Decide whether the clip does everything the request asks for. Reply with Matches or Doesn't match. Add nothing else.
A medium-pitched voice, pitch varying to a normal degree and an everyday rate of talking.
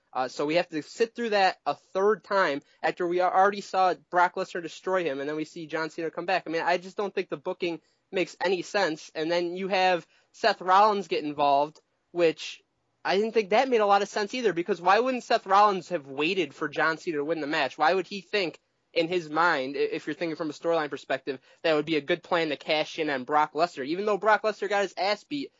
Doesn't match